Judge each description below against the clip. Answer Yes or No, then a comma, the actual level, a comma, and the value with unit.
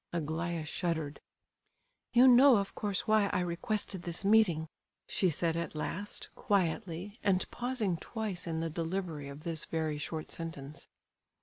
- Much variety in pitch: No, average, 4.0 semitones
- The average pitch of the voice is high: No, medium, 170 Hz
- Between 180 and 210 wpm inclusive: No, average, 140 wpm